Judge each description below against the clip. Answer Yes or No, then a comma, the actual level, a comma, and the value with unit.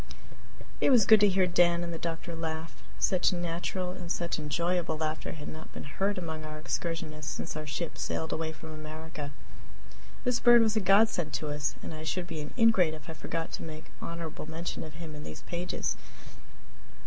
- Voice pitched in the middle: Yes, medium, 165 Hz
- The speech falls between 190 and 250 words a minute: Yes, average, 195 wpm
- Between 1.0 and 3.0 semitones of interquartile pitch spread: Yes, narrow, 2.4 semitones